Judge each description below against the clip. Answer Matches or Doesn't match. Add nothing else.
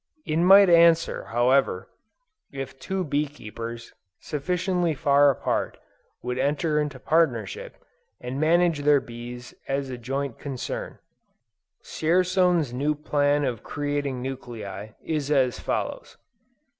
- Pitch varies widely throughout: Doesn't match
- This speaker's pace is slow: Matches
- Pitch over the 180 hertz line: Doesn't match